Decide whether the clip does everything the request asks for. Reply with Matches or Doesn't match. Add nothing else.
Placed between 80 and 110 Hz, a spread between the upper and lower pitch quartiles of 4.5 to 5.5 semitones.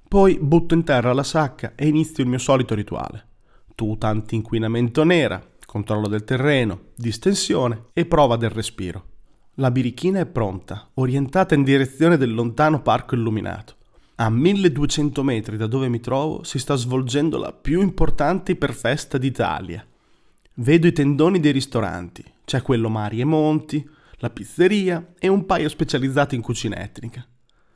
Doesn't match